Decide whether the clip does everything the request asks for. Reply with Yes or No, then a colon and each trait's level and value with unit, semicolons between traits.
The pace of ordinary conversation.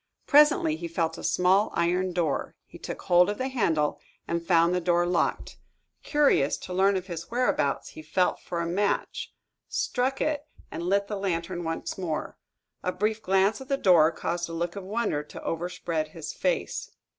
Yes: average, 180 wpm